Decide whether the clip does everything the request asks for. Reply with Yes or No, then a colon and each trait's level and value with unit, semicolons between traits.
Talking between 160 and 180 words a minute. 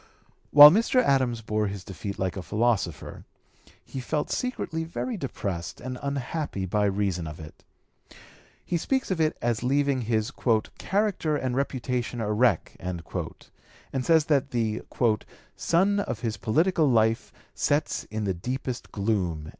No: average, 140 wpm